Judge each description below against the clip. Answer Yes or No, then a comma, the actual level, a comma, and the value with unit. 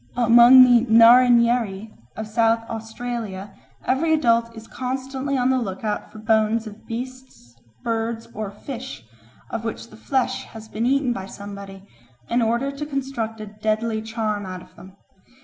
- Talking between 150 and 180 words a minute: Yes, average, 155 wpm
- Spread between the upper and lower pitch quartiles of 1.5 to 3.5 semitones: Yes, narrow, 2.5 semitones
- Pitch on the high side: Yes, high, 230 Hz